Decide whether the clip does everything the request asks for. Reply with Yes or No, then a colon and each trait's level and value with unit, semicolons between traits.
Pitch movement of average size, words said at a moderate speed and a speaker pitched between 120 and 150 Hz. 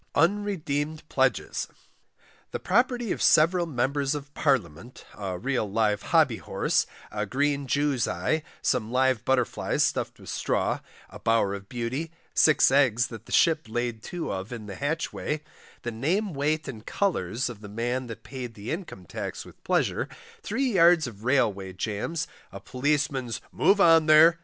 No: wide, 5.7 semitones; average, 155 wpm; low, 135 Hz